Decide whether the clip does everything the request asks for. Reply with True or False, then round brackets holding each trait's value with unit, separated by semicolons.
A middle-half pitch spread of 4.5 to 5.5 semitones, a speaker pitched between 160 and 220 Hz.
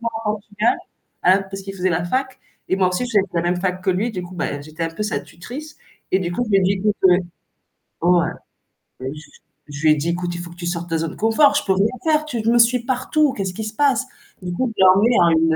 True (5.0 semitones; 190 Hz)